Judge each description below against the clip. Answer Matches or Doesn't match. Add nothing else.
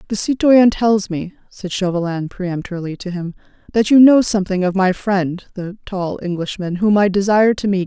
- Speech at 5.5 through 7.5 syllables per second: Doesn't match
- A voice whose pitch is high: Matches